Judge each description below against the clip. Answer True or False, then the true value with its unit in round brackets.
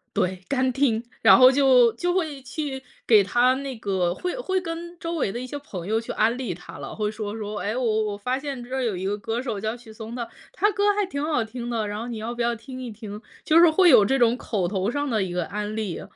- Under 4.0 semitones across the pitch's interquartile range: False (4.4 semitones)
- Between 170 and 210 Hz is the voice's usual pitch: False (235 Hz)